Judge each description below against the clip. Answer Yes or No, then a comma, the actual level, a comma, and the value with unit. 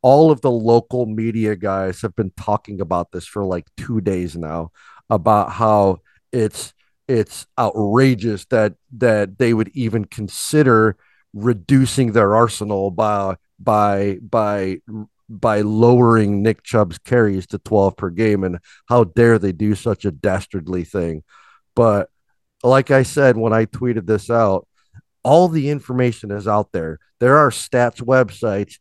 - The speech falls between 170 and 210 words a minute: No, average, 145 wpm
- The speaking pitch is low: Yes, low, 110 Hz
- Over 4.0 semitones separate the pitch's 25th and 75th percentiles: No, average, 3.5 semitones